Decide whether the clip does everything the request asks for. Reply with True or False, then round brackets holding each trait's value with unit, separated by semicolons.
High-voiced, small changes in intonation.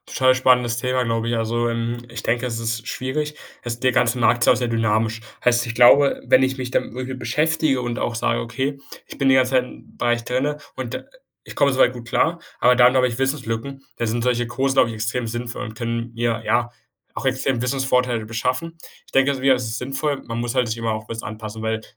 False (120 Hz; 2.1 semitones)